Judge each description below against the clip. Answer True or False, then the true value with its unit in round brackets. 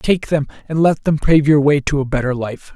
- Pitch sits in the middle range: True (145 Hz)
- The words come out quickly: True (260 wpm)